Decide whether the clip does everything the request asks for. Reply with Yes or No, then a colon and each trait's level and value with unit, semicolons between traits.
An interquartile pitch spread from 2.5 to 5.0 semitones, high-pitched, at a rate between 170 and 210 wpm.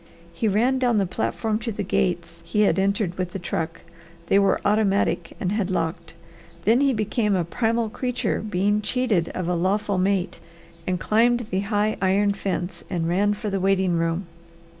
Yes: average, 3.1 semitones; high, 200 Hz; average, 180 wpm